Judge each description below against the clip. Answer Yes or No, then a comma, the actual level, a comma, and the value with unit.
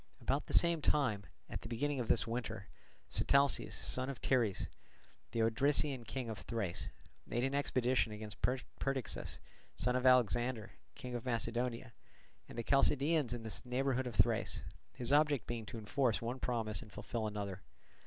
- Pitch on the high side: No, low, 120 Hz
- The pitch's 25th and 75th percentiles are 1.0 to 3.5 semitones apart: Yes, average, 2.9 semitones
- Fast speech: No, average, 160 wpm